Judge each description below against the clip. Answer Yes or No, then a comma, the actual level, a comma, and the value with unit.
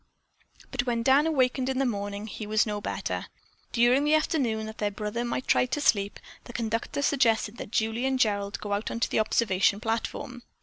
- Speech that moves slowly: No, average, 190 wpm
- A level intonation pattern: No, average, 3.5 semitones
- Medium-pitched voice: No, high, 230 Hz